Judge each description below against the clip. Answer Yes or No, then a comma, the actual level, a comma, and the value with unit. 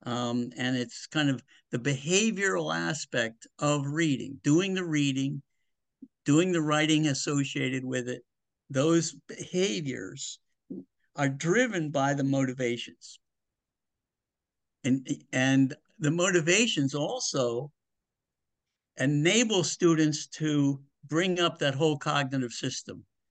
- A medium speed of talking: No, slow, 105 wpm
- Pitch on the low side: No, medium, 145 Hz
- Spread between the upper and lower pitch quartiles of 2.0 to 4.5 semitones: Yes, average, 4.1 semitones